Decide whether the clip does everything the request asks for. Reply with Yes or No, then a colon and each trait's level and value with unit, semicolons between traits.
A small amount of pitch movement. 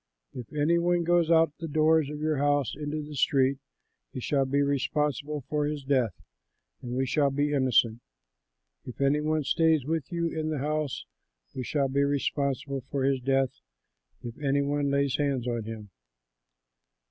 Yes: narrow, 2.2 semitones